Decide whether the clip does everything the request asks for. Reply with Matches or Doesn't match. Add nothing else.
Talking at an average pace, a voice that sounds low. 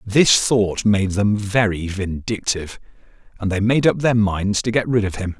Matches